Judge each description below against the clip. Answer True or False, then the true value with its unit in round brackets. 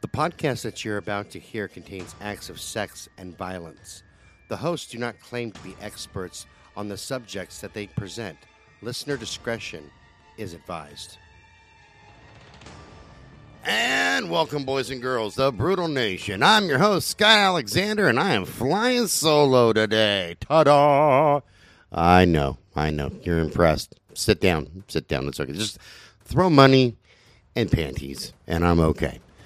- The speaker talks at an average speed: True (145 wpm)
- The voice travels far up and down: True (7.1 semitones)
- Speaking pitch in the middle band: False (105 Hz)